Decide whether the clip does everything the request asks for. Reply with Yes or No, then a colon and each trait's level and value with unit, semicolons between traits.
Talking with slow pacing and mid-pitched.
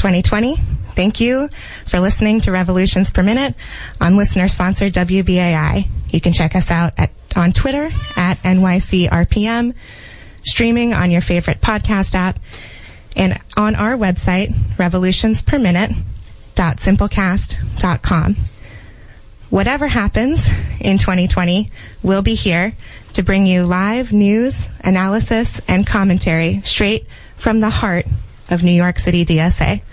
Yes: slow, 115 wpm; medium, 180 Hz